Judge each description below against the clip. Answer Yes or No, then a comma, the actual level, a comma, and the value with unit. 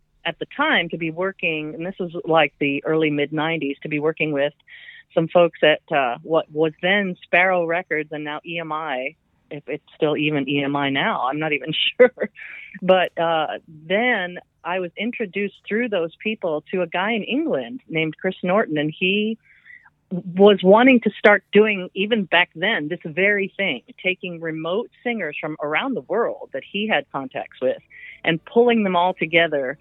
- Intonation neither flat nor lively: Yes, average, 4.6 semitones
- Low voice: No, medium, 180 Hz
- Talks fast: No, average, 175 wpm